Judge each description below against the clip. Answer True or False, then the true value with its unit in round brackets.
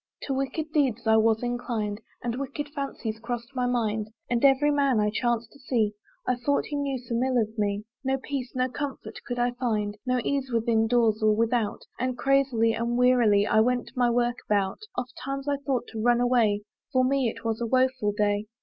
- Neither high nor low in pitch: False (245 Hz)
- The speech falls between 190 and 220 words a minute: True (205 wpm)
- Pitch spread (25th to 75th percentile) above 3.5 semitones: False (2.9 semitones)